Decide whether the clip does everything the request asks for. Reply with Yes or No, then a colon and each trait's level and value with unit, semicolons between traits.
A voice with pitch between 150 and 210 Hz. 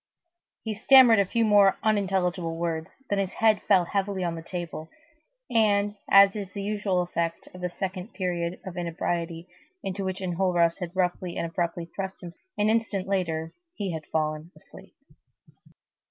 Yes: medium, 185 Hz